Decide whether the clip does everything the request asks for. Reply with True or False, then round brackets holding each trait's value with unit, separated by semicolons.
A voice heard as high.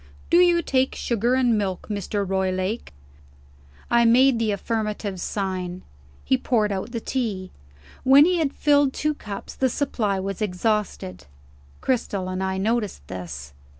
True (215 Hz)